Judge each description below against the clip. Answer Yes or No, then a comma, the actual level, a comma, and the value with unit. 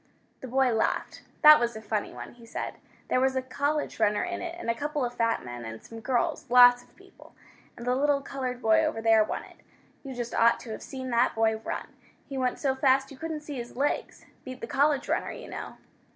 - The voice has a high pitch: Yes, very high, 250 Hz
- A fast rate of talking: Yes, fast, 230 wpm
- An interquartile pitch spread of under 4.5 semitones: Yes, average, 3.1 semitones